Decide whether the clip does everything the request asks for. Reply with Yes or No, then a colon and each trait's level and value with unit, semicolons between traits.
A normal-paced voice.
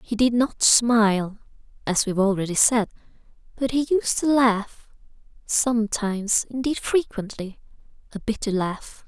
No: slow, 130 wpm